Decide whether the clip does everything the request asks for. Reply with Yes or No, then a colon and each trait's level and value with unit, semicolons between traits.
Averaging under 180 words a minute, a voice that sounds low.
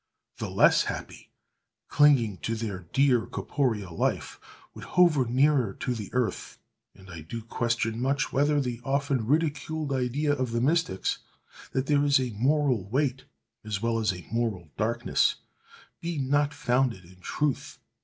Yes: average, 150 wpm; low, 125 Hz